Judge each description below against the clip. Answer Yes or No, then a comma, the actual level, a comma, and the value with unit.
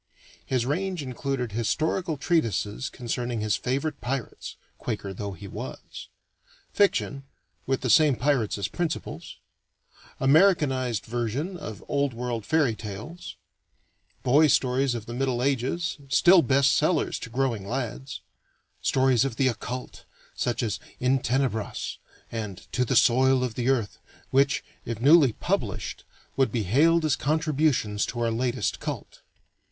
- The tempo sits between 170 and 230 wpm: No, slow, 135 wpm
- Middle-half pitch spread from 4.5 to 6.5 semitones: No, average, 3.4 semitones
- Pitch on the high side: No, low, 130 Hz